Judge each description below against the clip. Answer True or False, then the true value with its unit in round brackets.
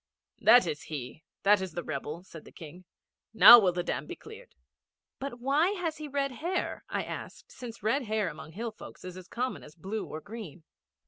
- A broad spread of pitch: True (7.6 semitones)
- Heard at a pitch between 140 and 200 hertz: False (215 Hz)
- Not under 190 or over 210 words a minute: True (200 wpm)